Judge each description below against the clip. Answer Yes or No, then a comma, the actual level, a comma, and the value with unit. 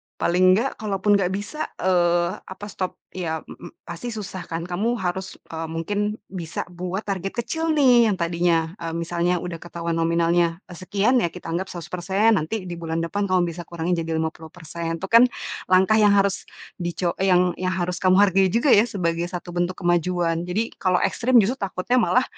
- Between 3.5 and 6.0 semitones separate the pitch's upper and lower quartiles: No, average, 2.9 semitones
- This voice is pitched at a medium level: Yes, medium, 180 Hz